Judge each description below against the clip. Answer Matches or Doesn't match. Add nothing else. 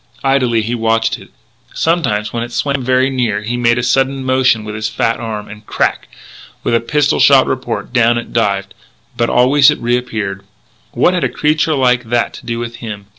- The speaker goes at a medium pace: Matches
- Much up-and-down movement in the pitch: Doesn't match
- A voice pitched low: Matches